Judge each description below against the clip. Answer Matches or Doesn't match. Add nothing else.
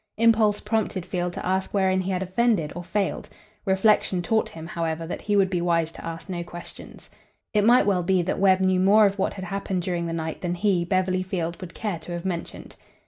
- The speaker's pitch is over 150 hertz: Matches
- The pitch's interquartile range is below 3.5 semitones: Matches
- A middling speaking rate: Doesn't match